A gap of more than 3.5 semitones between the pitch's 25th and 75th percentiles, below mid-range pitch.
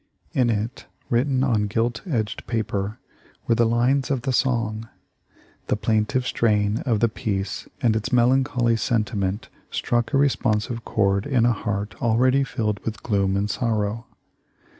No: narrow, 2.6 semitones; low, 115 Hz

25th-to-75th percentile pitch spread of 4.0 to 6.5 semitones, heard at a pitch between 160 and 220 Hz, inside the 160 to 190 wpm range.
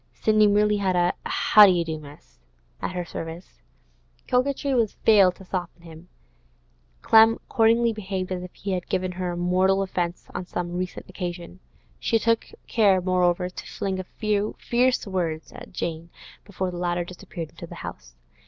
No: average, 3.1 semitones; medium, 185 Hz; average, 170 wpm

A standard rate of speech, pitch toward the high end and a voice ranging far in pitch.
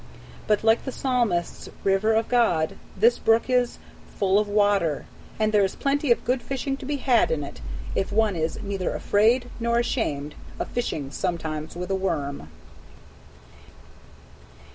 Yes: average, 155 wpm; high, 210 Hz; wide, 5.7 semitones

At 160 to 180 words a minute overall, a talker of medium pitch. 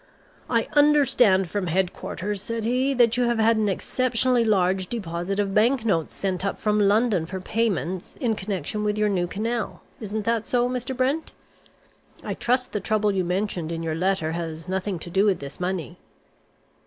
No: average, 175 wpm; high, 205 Hz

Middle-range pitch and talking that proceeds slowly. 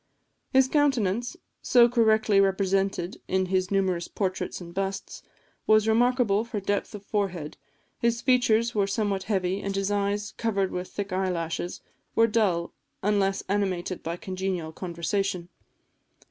No: high, 195 Hz; slow, 130 wpm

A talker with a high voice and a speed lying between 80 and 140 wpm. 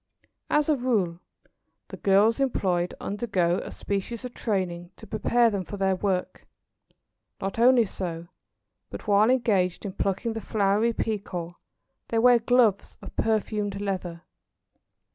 Yes: high, 205 Hz; slow, 135 wpm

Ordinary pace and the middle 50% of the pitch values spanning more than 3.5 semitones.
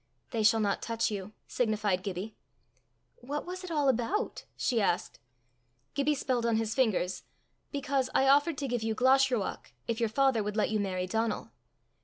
Yes: average, 170 wpm; average, 4.2 semitones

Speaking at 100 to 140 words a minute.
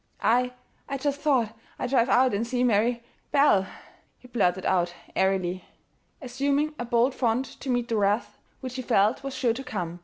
No: average, 180 wpm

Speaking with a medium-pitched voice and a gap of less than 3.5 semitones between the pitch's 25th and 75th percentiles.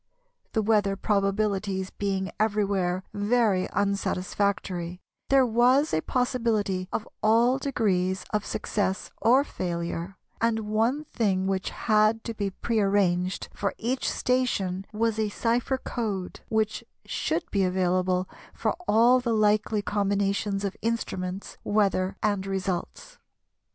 No: high, 205 Hz; average, 3.1 semitones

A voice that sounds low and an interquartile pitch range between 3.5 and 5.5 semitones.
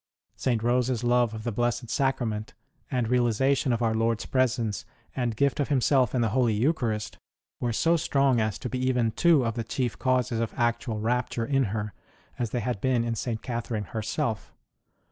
No: low, 120 Hz; narrow, 2.4 semitones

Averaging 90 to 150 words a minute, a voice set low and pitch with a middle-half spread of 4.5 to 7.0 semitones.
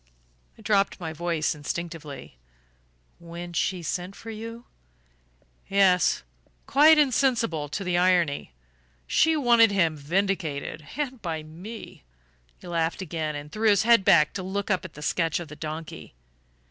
No: average, 145 wpm; medium, 175 Hz; average, 5.1 semitones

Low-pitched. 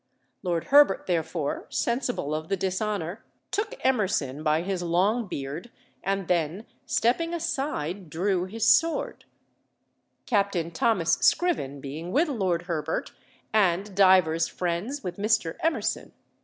No: high, 190 Hz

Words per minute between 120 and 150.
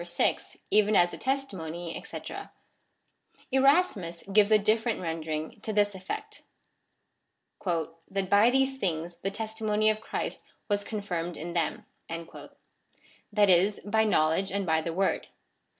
Yes: average, 145 wpm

